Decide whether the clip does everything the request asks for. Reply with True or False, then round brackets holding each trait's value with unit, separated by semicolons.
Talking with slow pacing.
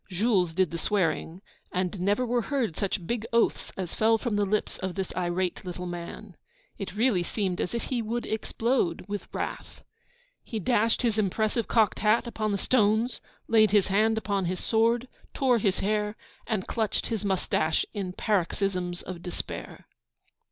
False (165 wpm)